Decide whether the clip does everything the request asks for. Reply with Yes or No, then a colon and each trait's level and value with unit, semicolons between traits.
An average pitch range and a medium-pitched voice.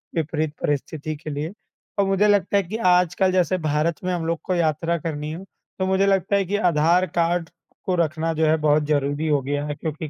Yes: average, 3.3 semitones; medium, 165 Hz